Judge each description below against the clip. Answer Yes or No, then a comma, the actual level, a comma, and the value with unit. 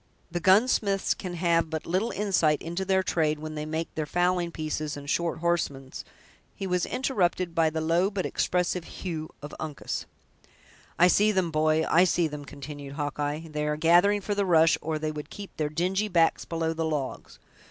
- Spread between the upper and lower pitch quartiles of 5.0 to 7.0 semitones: No, average, 2.9 semitones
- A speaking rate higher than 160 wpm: Yes, average, 185 wpm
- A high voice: No, medium, 165 Hz